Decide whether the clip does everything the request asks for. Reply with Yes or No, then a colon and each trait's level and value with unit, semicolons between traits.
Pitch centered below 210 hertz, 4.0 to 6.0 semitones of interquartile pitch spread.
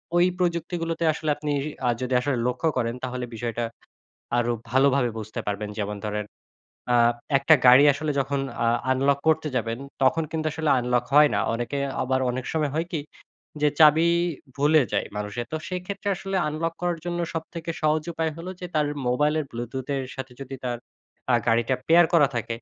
Yes: medium, 140 Hz; average, 4.6 semitones